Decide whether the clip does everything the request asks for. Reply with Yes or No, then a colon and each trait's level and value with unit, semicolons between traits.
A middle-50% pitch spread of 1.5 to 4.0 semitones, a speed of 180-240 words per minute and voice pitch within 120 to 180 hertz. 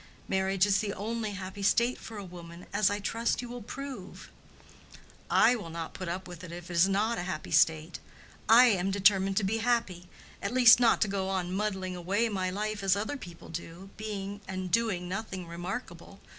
No: average, 3.1 semitones; average, 195 wpm; high, 195 Hz